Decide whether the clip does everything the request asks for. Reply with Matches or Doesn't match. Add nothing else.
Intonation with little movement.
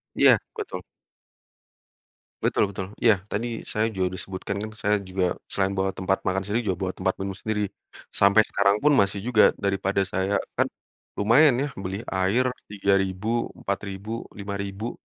Matches